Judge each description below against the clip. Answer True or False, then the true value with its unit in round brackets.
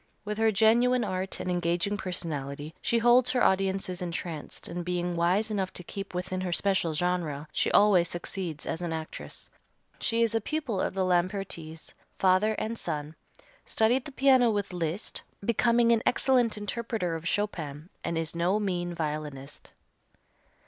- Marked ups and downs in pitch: False (4.5 semitones)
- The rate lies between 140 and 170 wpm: True (155 wpm)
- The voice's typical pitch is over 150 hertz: True (185 Hz)